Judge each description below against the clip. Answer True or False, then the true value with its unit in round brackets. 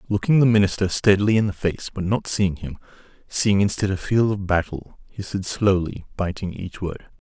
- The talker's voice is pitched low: True (100 Hz)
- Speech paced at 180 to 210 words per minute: True (190 wpm)